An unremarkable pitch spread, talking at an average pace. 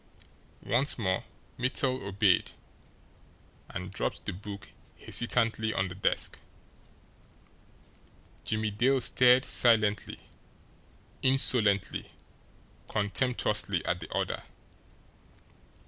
No: average, 3.8 semitones; slow, 80 wpm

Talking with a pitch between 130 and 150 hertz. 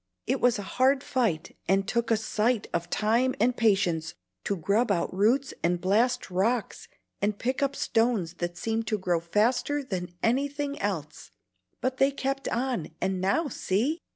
No: high, 225 Hz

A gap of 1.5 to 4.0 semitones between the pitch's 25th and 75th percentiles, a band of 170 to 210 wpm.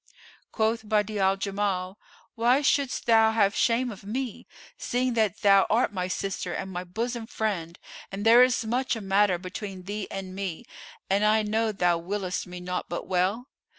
Yes: average, 3.0 semitones; average, 175 wpm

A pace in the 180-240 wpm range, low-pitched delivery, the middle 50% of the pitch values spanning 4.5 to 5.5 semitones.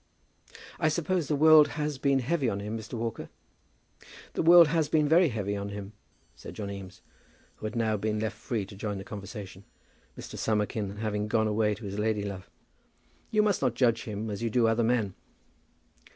Yes: average, 190 wpm; low, 110 Hz; average, 5.1 semitones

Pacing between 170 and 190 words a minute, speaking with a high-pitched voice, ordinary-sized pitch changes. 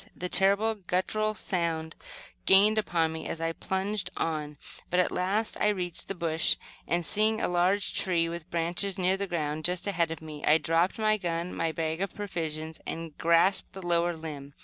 No: average, 185 wpm; medium, 175 Hz; average, 3.0 semitones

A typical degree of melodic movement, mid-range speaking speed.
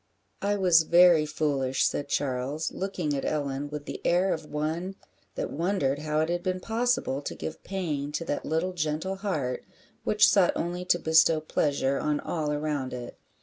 Yes: average, 3.7 semitones; average, 175 wpm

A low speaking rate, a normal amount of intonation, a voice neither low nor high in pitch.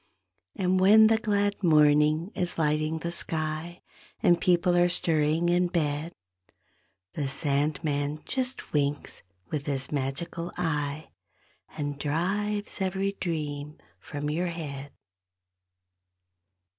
Yes: slow, 105 wpm; average, 3.3 semitones; medium, 160 Hz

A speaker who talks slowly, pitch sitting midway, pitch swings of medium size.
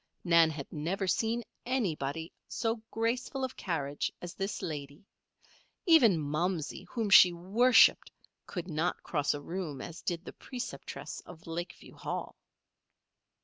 No: slow, 130 wpm; medium, 175 Hz; wide, 6.0 semitones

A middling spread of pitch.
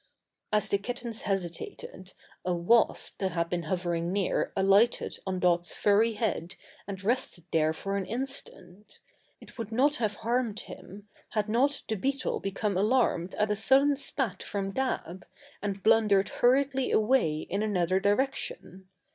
Yes: average, 4.1 semitones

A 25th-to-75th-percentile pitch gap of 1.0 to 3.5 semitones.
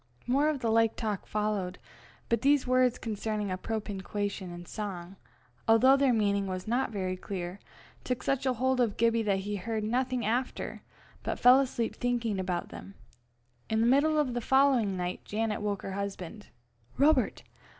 No: average, 4.0 semitones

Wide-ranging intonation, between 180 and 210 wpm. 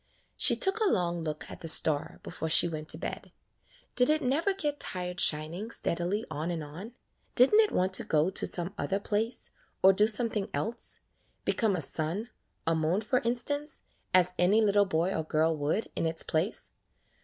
Yes: wide, 5.9 semitones; average, 190 wpm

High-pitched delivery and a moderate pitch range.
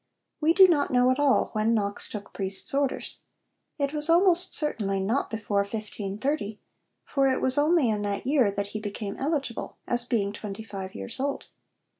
No: high, 230 Hz; wide, 5.8 semitones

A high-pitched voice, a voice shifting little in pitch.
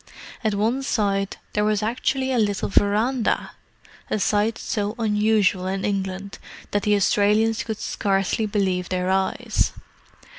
Yes: high, 205 Hz; narrow, 2.0 semitones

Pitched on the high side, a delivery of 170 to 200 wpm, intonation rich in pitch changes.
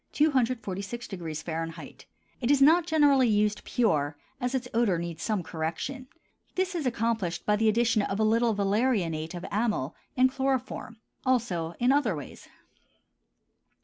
No: high, 220 Hz; average, 140 wpm; wide, 6.9 semitones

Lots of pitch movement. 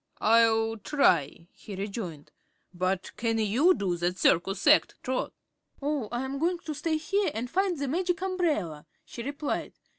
Yes: wide, 8.0 semitones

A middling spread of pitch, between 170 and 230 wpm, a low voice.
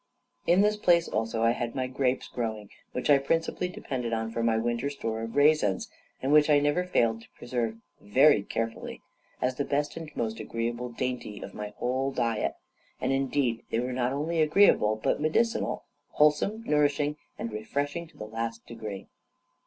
Yes: average, 4.5 semitones; average, 175 wpm; low, 125 Hz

